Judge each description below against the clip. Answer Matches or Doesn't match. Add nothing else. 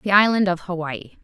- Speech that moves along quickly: Doesn't match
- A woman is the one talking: Matches